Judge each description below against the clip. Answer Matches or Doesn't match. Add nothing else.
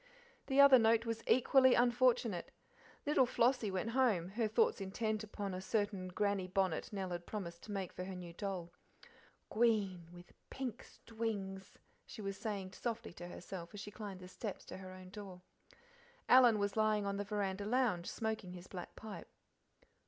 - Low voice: Doesn't match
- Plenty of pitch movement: Doesn't match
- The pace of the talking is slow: Doesn't match